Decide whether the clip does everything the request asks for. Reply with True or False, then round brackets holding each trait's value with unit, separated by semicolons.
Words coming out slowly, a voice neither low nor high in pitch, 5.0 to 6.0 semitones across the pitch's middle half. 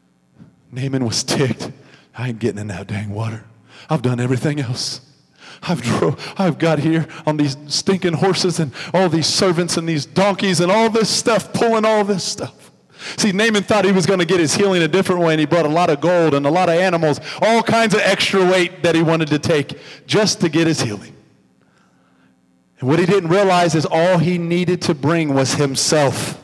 False (205 wpm; 165 Hz; 5.3 semitones)